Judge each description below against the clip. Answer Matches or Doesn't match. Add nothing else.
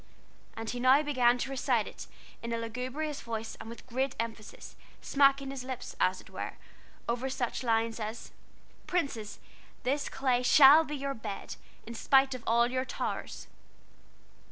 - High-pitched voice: Matches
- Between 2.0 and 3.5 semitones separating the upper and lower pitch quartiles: Matches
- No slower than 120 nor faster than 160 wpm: Matches